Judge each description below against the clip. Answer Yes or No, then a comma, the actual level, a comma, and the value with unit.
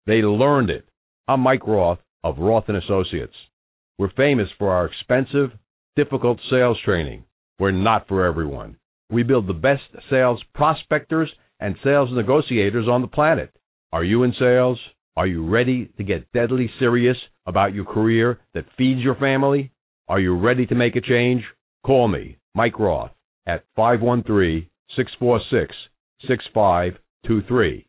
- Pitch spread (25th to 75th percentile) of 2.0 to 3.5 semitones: No, average, 4.6 semitones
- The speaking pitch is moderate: No, low, 120 Hz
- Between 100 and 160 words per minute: Yes, average, 145 wpm